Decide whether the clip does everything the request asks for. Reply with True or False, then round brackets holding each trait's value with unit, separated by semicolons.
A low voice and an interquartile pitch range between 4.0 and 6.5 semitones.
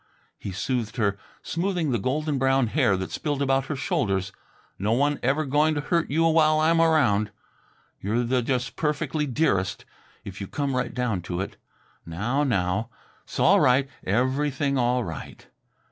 True (130 Hz; 5.6 semitones)